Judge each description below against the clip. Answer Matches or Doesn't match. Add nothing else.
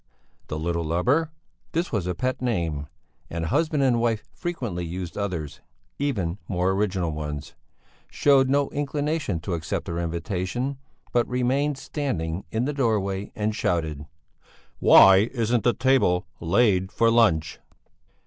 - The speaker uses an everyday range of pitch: Doesn't match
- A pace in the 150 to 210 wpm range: Doesn't match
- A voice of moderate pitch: Doesn't match